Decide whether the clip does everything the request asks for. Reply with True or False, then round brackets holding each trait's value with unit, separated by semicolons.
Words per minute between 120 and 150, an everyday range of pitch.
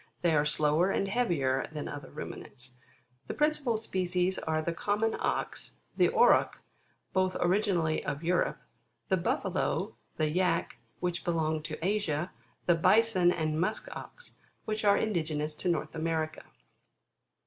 True (140 wpm; 3.9 semitones)